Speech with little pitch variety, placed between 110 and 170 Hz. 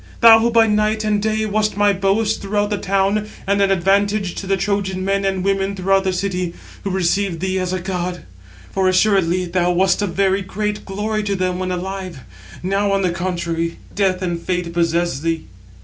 No: narrow, 1.9 semitones; high, 195 Hz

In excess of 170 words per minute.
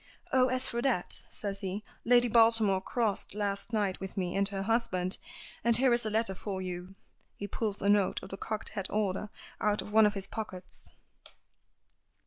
Yes: average, 185 wpm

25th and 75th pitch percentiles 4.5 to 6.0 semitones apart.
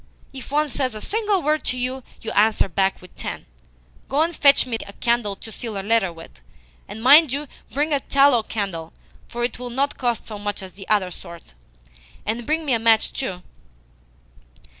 Yes: wide, 5.4 semitones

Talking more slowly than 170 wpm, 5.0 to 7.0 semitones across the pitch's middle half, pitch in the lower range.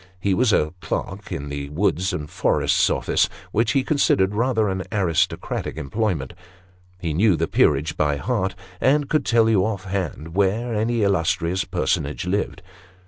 Yes: average, 160 wpm; wide, 5.4 semitones; very low, 95 Hz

